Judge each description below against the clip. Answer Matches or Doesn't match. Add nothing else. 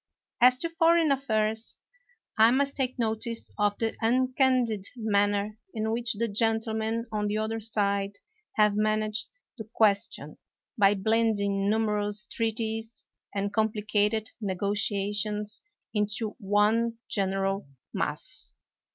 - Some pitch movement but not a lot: Doesn't match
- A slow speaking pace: Matches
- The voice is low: Doesn't match